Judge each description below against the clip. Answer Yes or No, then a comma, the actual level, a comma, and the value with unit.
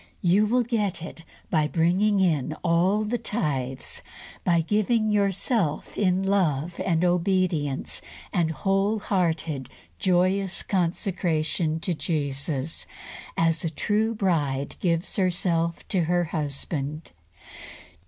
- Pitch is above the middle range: No, medium, 175 Hz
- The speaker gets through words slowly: Yes, slow, 105 wpm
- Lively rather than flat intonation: No, average, 3.7 semitones